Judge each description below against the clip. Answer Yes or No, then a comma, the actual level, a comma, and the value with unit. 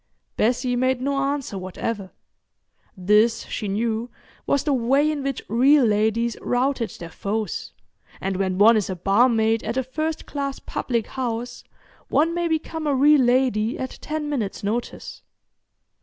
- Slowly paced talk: No, average, 150 wpm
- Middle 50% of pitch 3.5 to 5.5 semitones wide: Yes, average, 4.2 semitones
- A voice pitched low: No, high, 245 Hz